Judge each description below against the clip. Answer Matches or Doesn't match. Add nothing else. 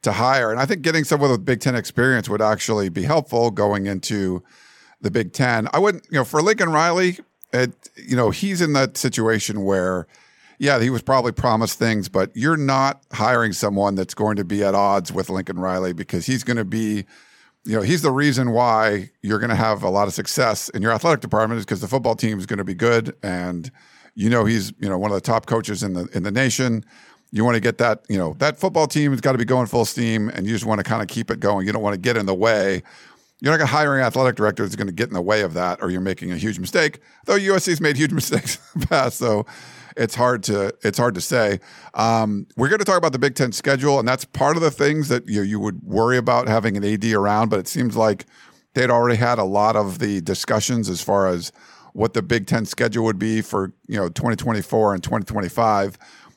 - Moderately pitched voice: Doesn't match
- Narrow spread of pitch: Doesn't match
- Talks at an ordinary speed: Doesn't match